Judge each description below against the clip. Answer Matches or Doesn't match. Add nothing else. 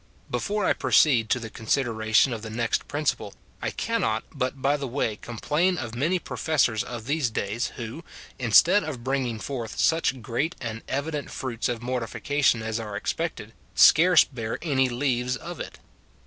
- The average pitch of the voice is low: Matches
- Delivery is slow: Doesn't match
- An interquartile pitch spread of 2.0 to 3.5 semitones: Doesn't match